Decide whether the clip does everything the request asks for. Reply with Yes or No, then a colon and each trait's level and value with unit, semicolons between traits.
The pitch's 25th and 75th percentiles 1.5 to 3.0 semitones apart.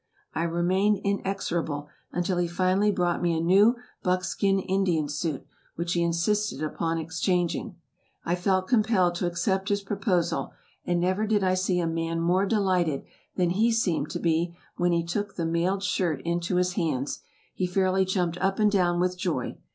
Yes: narrow, 2.4 semitones